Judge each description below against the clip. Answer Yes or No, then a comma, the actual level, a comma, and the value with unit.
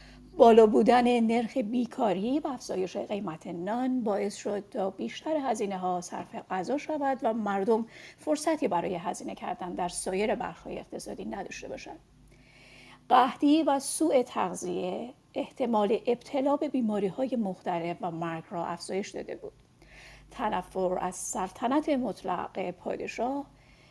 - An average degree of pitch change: No, wide, 6.0 semitones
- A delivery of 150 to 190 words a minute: No, average, 125 wpm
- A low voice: No, high, 220 Hz